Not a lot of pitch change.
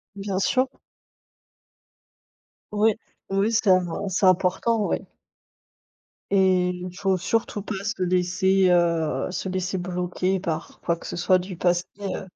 Yes: narrow, 1.6 semitones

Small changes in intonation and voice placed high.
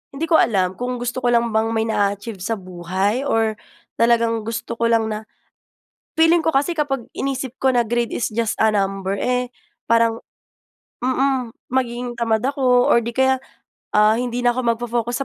Yes: narrow, 2.3 semitones; high, 235 Hz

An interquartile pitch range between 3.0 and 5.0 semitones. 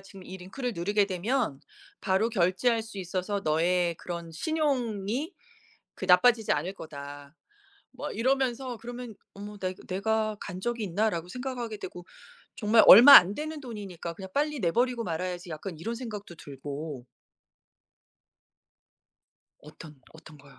No: wide, 5.5 semitones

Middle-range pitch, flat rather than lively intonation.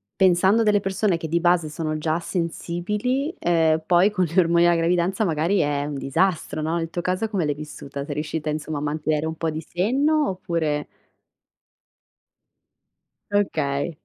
No: medium, 170 Hz; average, 3.4 semitones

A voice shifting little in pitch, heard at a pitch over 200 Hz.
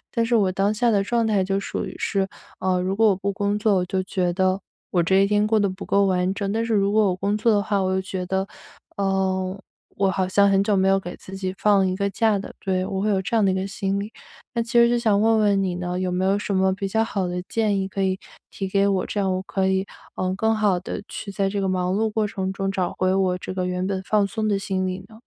No: narrow, 1.6 semitones; high, 195 Hz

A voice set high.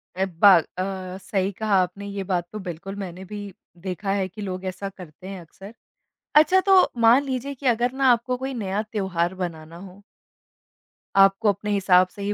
Yes: high, 195 Hz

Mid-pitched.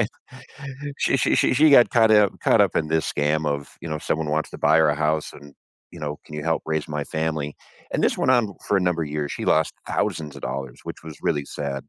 No: very low, 80 Hz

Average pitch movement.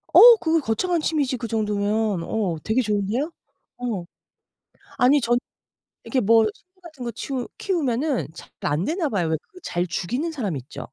No: wide, 6.6 semitones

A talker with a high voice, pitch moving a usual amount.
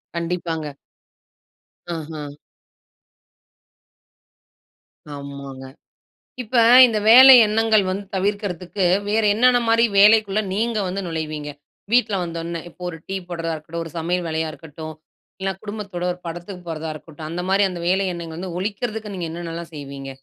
No: medium, 175 Hz; average, 4.1 semitones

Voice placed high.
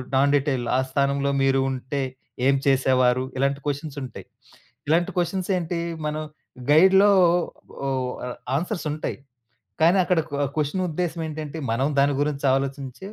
No: medium, 145 Hz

